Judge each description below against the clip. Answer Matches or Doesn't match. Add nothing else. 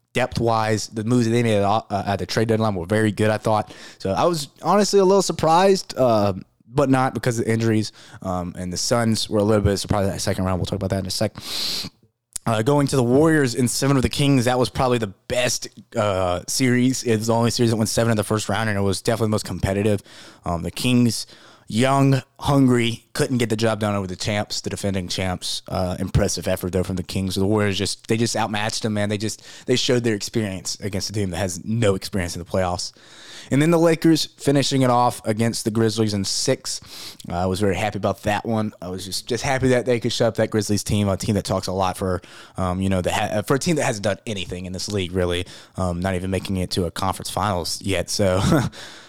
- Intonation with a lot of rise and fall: Doesn't match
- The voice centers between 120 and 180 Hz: Doesn't match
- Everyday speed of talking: Doesn't match